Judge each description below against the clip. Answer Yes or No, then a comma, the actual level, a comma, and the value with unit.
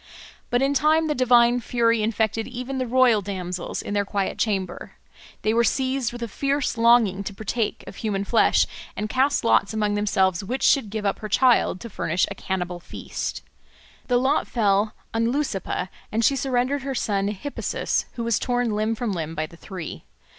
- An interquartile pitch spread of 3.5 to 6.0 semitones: Yes, average, 3.8 semitones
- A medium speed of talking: Yes, average, 185 wpm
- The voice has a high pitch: Yes, high, 225 Hz